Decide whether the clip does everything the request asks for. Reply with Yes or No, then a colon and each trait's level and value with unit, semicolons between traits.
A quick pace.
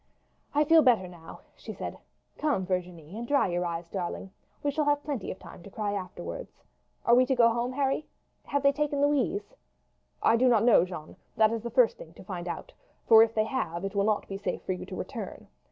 Yes: fast, 220 wpm